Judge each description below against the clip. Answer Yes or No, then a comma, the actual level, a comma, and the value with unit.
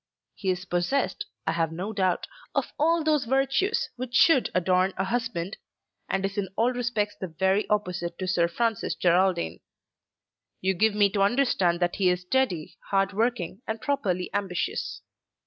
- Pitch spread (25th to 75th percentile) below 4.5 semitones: No, average, 4.9 semitones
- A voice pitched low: No, high, 195 Hz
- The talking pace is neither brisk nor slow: Yes, average, 165 wpm